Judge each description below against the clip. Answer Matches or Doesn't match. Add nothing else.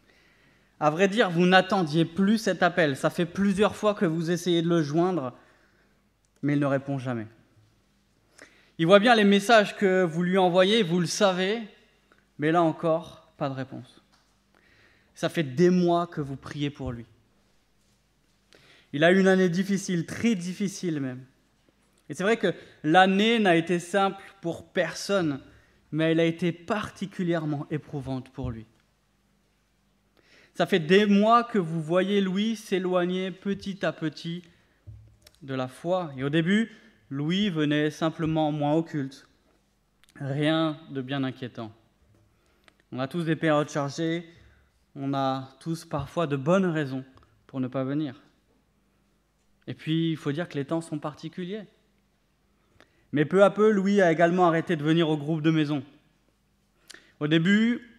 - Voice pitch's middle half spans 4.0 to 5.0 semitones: Matches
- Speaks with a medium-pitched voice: Matches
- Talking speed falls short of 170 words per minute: Matches